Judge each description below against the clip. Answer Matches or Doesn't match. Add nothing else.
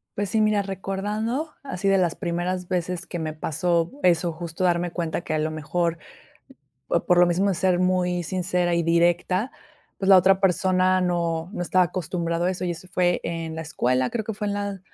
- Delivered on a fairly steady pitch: Matches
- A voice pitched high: Doesn't match